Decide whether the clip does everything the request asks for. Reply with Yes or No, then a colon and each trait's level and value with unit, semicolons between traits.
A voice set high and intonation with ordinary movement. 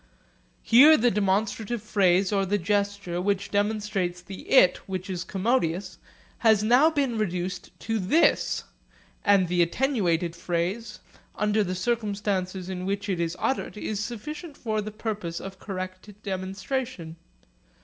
Yes: high, 200 Hz; average, 3.0 semitones